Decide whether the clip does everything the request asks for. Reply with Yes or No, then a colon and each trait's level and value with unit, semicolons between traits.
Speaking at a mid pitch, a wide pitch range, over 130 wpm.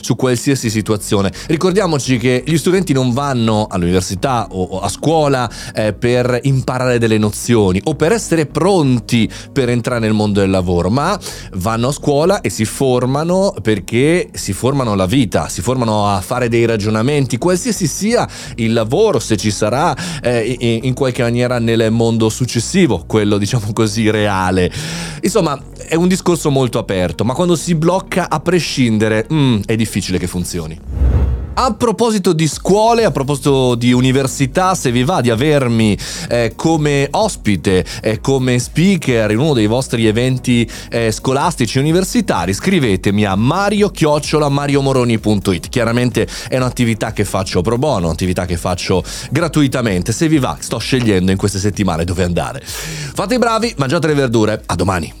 No: low, 125 Hz; wide, 5.7 semitones; average, 155 wpm